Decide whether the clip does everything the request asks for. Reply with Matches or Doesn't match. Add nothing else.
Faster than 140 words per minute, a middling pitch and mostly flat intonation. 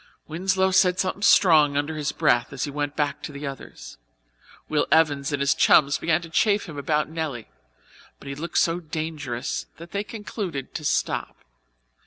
Doesn't match